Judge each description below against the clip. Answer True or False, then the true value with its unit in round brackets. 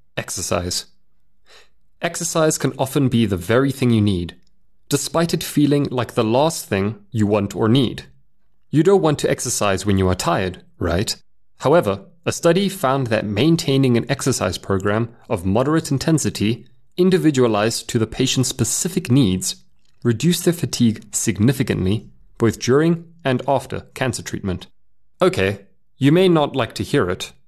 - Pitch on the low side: True (120 Hz)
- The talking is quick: False (145 wpm)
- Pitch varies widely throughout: True (5.9 semitones)